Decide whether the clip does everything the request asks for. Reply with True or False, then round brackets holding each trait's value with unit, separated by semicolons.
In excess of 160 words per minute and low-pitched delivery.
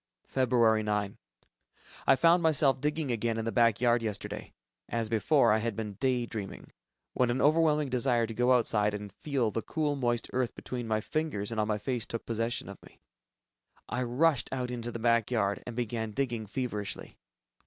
True (185 wpm; 120 Hz)